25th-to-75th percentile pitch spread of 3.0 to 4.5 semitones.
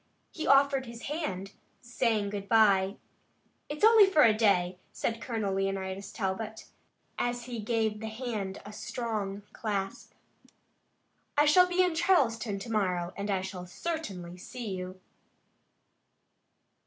Yes: average, 4.0 semitones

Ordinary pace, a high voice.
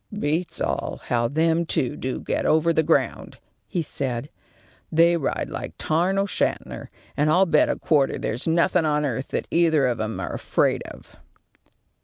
No: average, 165 wpm; medium, 155 Hz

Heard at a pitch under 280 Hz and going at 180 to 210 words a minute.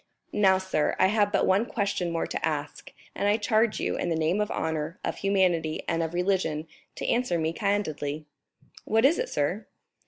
Yes: medium, 185 Hz; average, 190 wpm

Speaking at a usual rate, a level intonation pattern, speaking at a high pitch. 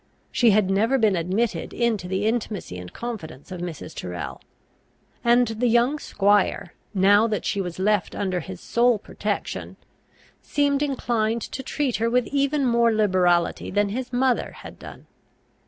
No: average, 155 wpm; average, 4.3 semitones; high, 215 Hz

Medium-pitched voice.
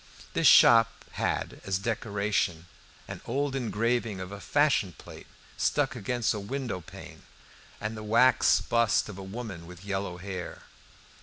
No: low, 105 Hz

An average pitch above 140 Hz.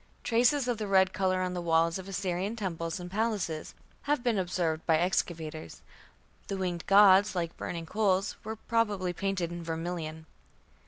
Yes: medium, 185 Hz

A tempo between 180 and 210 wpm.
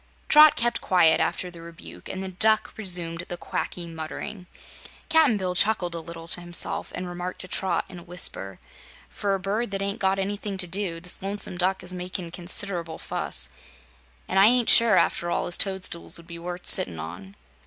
Yes: average, 190 wpm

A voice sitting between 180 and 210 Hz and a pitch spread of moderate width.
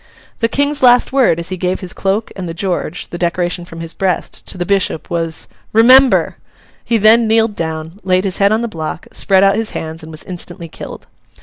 Yes: medium, 185 Hz; average, 4.6 semitones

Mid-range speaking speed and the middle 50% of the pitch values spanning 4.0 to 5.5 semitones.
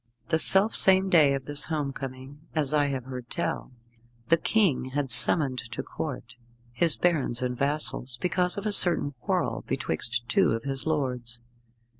Yes: average, 165 wpm; average, 4.3 semitones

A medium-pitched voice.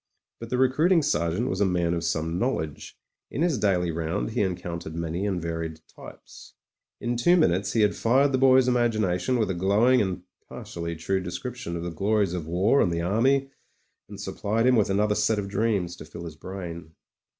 No: very low, 95 Hz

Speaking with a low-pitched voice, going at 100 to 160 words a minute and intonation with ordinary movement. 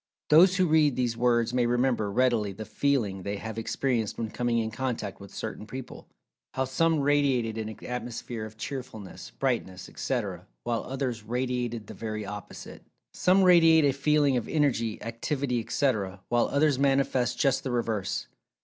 Yes: low, 120 Hz; average, 155 wpm; average, 3.8 semitones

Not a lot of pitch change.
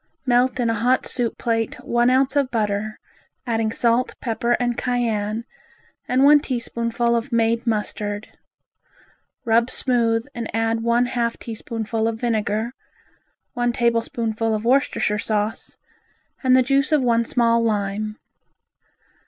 Yes: narrow, 1.6 semitones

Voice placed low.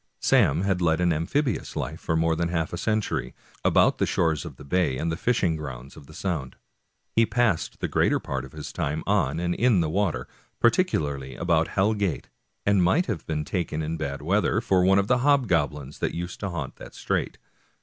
Yes: very low, 85 Hz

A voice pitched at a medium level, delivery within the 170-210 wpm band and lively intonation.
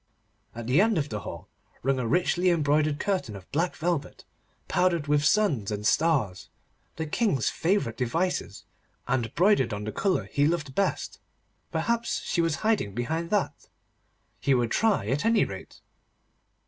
No: medium, 150 Hz; average, 155 wpm; wide, 7.0 semitones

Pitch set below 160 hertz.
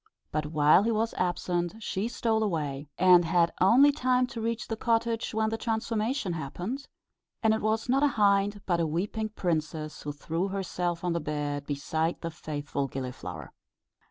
No: medium, 180 Hz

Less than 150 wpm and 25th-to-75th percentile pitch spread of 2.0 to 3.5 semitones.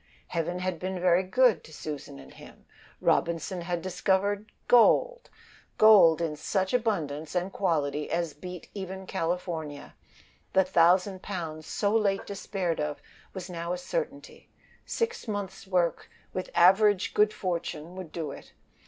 Yes: average, 140 wpm; average, 3.1 semitones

